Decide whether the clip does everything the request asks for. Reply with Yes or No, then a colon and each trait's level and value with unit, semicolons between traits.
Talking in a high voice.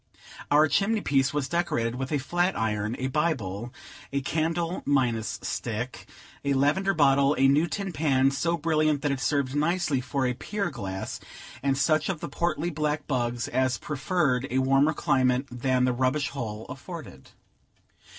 No: medium, 140 Hz